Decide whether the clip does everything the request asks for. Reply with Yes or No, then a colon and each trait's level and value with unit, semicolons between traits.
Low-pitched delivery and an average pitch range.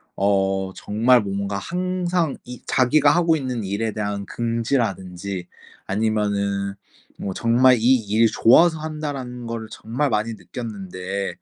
Yes: low, 115 Hz; average, 4.5 semitones